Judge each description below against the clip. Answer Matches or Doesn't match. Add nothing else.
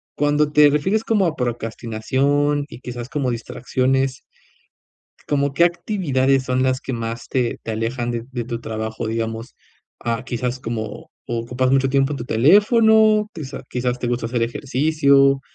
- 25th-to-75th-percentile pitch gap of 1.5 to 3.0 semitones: Doesn't match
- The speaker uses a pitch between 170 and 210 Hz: Doesn't match